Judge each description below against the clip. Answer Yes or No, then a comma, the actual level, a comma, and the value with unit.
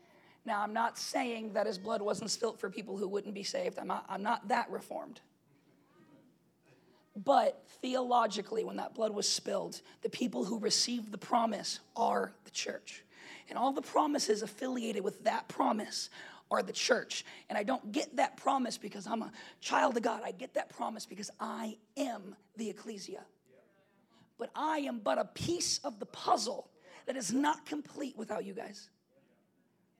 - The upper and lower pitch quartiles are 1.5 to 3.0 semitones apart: No, average, 3.8 semitones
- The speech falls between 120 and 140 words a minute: No, average, 170 wpm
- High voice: Yes, high, 225 Hz